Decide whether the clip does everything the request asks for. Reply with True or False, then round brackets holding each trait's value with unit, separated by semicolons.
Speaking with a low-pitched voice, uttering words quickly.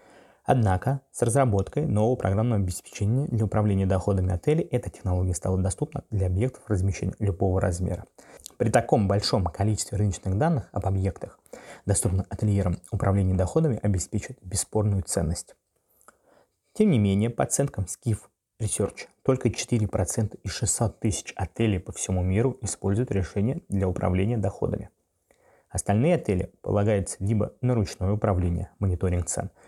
False (100 Hz; 130 wpm)